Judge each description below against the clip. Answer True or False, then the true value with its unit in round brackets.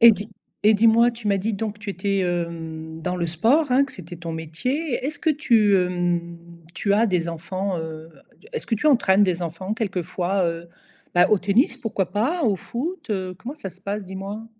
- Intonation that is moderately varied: True (4.4 semitones)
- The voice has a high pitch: True (195 Hz)